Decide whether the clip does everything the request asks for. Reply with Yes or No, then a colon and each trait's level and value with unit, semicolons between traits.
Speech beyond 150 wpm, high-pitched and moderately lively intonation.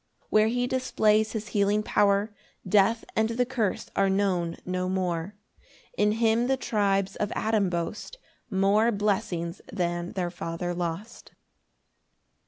No: slow, 135 wpm; high, 200 Hz; average, 3.2 semitones